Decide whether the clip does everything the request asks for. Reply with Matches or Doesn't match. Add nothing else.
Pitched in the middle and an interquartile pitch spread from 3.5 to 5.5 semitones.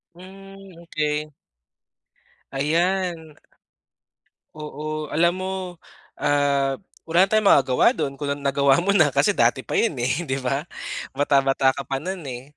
Matches